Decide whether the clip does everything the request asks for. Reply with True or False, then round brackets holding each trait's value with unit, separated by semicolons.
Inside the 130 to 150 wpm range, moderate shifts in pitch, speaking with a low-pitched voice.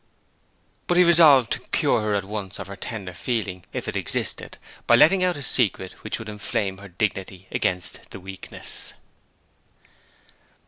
True (145 wpm; 4.7 semitones; 105 Hz)